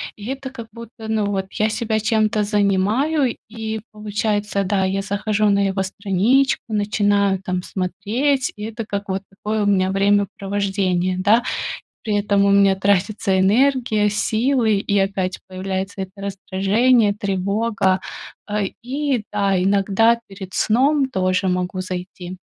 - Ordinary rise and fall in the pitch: No, narrow, 2.3 semitones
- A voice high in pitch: Yes, high, 205 Hz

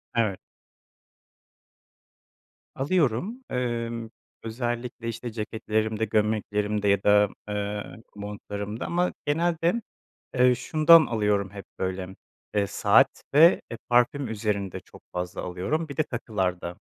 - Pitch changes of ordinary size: Yes, average, 3.6 semitones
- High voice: No, low, 110 Hz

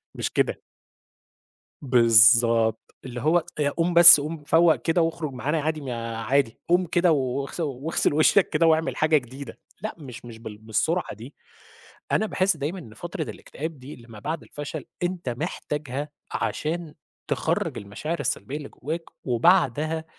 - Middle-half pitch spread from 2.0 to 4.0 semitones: No, average, 5.0 semitones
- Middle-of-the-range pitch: Yes, medium, 150 Hz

